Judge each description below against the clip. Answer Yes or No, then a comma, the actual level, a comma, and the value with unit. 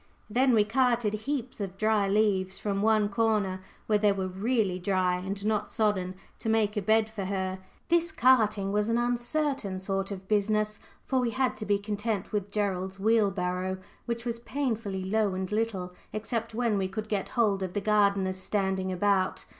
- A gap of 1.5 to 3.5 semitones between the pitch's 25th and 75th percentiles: Yes, average, 2.7 semitones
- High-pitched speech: Yes, high, 210 Hz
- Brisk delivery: No, average, 180 wpm